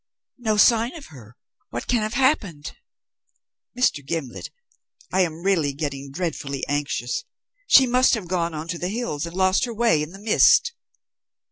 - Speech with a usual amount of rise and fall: No, wide, 7.8 semitones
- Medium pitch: Yes, medium, 180 Hz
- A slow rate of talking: No, average, 160 wpm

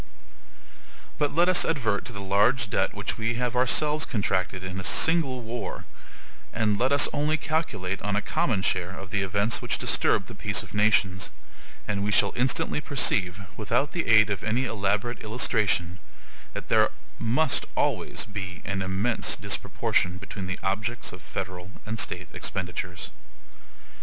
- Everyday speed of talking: Yes, average, 155 wpm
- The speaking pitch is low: Yes, low, 105 Hz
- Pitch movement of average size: Yes, average, 4.4 semitones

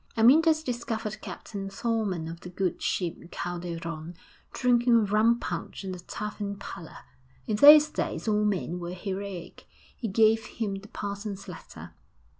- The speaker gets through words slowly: No, average, 145 wpm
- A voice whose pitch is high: Yes, high, 205 Hz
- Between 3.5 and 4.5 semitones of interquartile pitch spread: Yes, average, 3.9 semitones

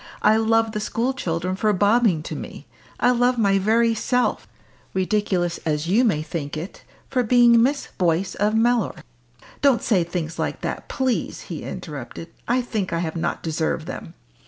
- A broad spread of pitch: Yes, wide, 5.7 semitones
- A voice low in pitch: No, high, 205 Hz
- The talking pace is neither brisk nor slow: Yes, average, 170 wpm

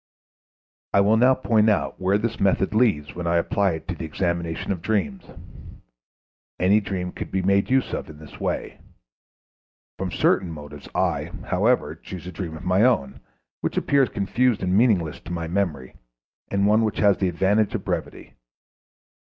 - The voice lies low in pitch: Yes, very low, 95 Hz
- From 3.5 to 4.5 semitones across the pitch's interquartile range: Yes, average, 3.9 semitones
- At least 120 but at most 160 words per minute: No, average, 170 wpm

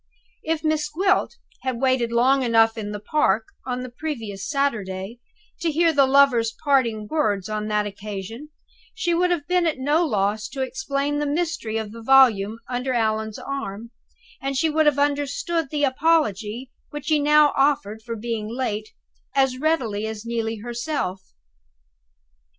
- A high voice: Yes, very high, 255 Hz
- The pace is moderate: Yes, average, 155 wpm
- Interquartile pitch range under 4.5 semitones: No, average, 5.2 semitones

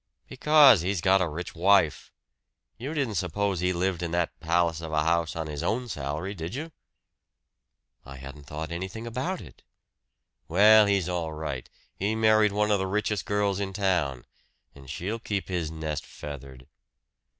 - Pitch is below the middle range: Yes, very low, 90 Hz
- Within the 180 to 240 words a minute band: No, average, 165 wpm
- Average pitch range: Yes, average, 4.6 semitones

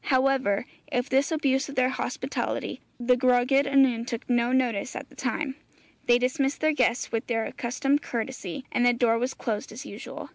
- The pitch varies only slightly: Yes, narrow, 2.2 semitones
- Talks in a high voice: Yes, very high, 255 Hz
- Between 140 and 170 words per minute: No, average, 180 wpm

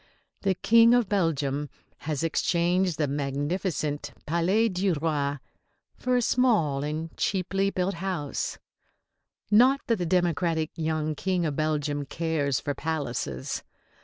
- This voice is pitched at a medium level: Yes, medium, 165 Hz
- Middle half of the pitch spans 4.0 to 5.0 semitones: Yes, average, 4.5 semitones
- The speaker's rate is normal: No, slow, 125 wpm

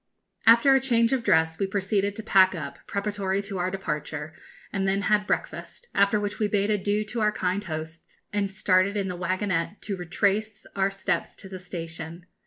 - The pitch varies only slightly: Yes, narrow, 2.3 semitones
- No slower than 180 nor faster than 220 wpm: Yes, average, 190 wpm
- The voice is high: Yes, high, 195 Hz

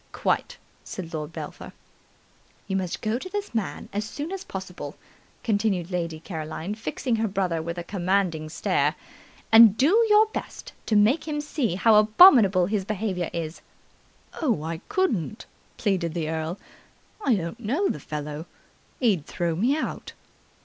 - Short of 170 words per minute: Yes, average, 150 wpm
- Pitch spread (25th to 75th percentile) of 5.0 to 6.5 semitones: Yes, wide, 5.6 semitones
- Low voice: No, high, 195 Hz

